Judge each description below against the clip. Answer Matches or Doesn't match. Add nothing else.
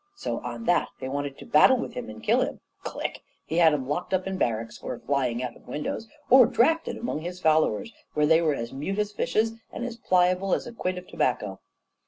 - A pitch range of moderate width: Doesn't match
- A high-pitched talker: Doesn't match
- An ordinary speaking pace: Doesn't match